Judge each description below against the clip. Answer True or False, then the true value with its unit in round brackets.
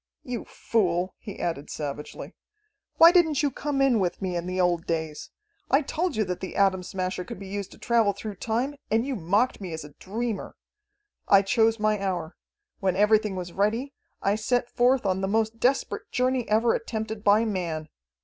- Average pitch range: True (4.3 semitones)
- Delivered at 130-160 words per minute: False (190 wpm)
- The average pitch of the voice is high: True (205 Hz)